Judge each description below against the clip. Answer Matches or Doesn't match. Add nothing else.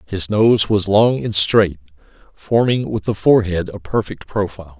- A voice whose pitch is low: Matches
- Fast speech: Doesn't match